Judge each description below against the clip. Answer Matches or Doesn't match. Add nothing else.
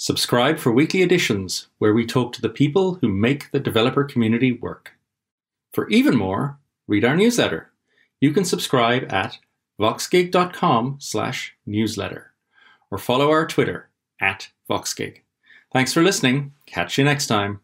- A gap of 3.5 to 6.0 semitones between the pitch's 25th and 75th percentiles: Matches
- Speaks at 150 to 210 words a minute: Doesn't match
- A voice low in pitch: Matches